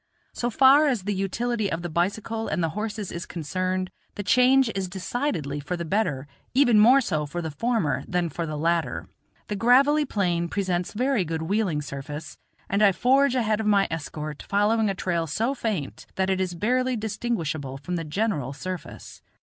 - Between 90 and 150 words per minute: No, average, 180 wpm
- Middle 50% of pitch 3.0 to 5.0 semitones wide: No, wide, 5.4 semitones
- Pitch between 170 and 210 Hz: Yes, high, 190 Hz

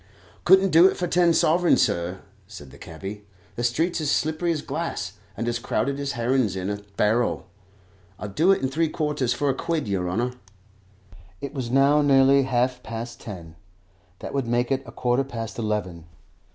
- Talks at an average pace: Yes, average, 185 wpm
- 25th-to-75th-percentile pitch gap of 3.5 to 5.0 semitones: No, wide, 5.6 semitones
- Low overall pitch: Yes, low, 125 Hz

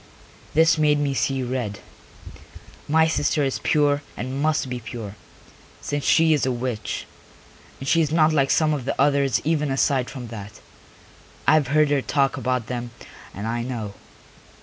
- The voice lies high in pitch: No, low, 135 Hz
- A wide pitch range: No, average, 3.4 semitones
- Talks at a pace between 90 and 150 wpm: No, average, 170 wpm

